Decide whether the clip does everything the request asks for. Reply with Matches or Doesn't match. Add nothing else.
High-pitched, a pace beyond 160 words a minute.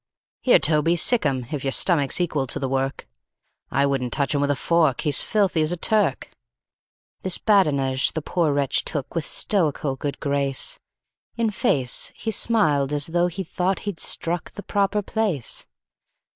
Doesn't match